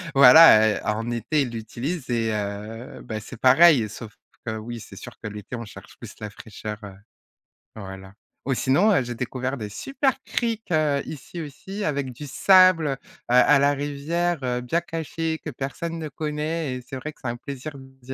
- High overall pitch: No, low, 135 Hz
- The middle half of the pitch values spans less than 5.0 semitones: No, average, 5.3 semitones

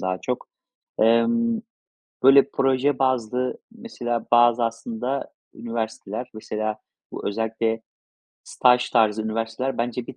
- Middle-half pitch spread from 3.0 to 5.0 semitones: No, narrow, 2.5 semitones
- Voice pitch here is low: Yes, low, 120 Hz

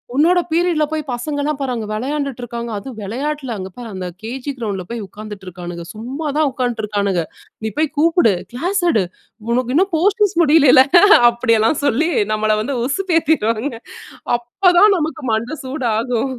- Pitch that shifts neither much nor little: No, wide, 5.9 semitones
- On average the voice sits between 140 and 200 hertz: No, very high, 255 Hz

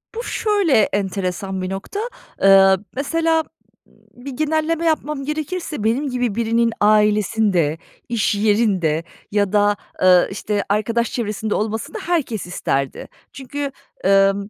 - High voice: Yes, high, 215 Hz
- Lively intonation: Yes, wide, 6.4 semitones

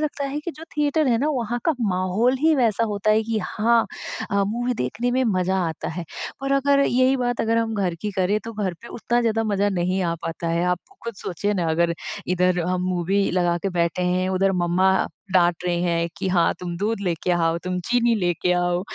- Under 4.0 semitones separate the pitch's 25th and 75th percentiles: No, average, 4.8 semitones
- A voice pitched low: No, high, 195 Hz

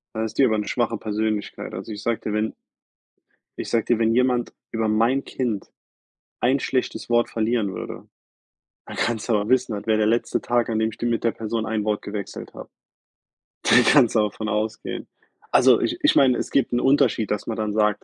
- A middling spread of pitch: No, narrow, 1.9 semitones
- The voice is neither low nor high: No, low, 110 Hz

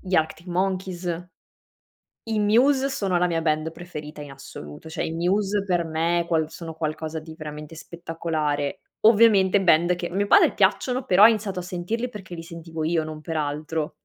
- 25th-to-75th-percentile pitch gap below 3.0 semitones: No, average, 3.3 semitones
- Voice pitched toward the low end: No, medium, 170 Hz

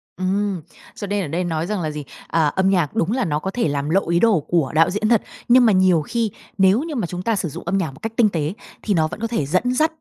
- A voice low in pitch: No, medium, 185 Hz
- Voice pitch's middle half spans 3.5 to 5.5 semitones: Yes, average, 4.8 semitones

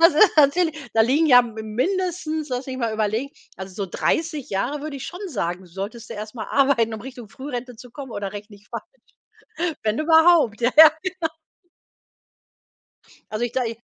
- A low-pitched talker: No, very high, 255 Hz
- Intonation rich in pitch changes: Yes, wide, 6.0 semitones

